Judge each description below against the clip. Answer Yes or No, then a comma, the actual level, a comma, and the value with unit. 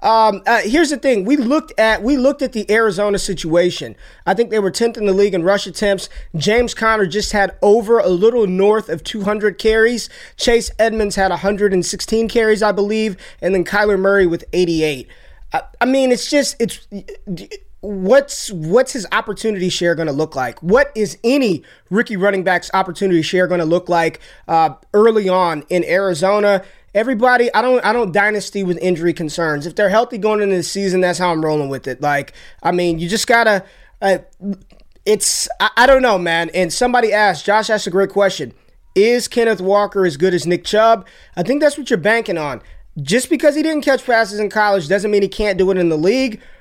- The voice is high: Yes, high, 205 Hz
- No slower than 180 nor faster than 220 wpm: Yes, average, 200 wpm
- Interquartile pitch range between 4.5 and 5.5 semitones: No, average, 3.9 semitones